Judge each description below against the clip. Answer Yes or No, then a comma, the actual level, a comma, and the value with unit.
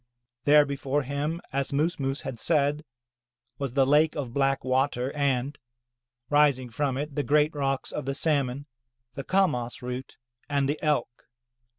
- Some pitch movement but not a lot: No, narrow, 1.9 semitones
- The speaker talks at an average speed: Yes, average, 155 wpm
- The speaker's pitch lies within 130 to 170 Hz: Yes, medium, 140 Hz